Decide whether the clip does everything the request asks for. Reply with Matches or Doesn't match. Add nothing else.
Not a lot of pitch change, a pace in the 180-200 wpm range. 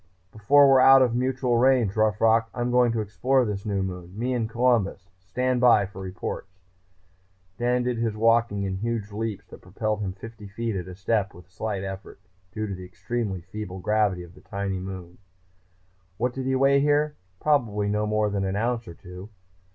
Doesn't match